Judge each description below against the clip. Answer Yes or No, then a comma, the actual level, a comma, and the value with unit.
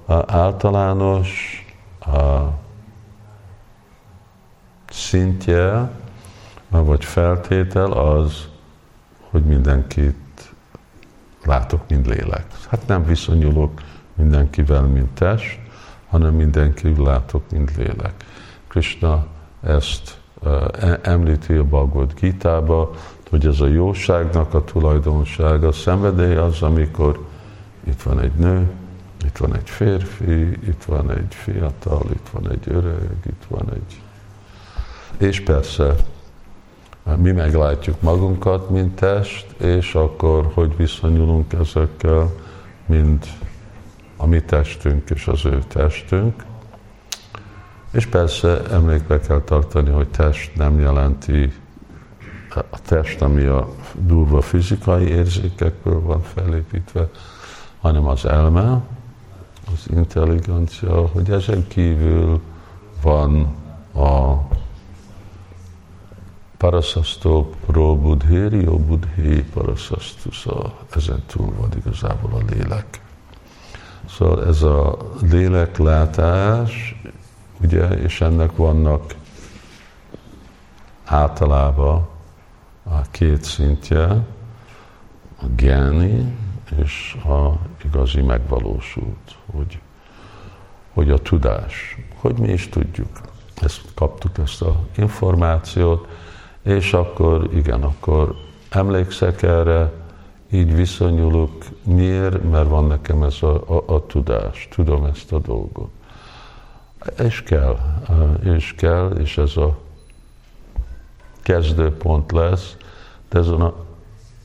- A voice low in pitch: Yes, very low, 85 Hz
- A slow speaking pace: Yes, slow, 95 wpm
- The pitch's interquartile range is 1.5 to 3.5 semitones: No, average, 4.1 semitones